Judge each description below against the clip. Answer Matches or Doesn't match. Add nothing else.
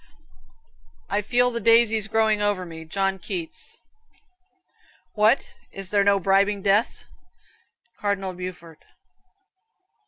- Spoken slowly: Matches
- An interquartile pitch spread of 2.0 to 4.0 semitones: Matches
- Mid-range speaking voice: Doesn't match